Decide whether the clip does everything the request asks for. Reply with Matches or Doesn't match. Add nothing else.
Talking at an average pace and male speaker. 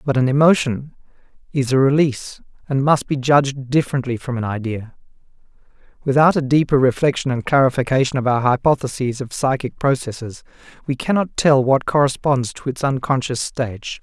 Matches